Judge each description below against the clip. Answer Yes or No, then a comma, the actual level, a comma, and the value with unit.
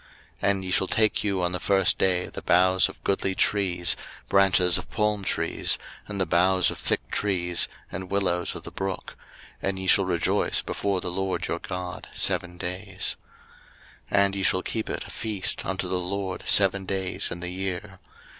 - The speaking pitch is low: Yes, very low, 95 Hz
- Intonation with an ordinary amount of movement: No, narrow, 1.4 semitones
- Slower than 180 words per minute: No, average, 185 wpm